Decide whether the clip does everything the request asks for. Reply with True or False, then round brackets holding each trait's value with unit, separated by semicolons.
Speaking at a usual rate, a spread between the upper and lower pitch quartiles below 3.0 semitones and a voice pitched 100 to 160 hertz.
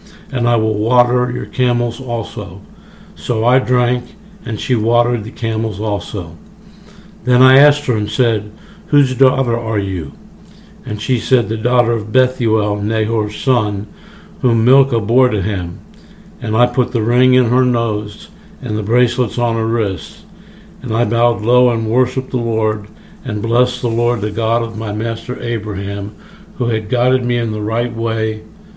True (165 wpm; 2.6 semitones; 120 Hz)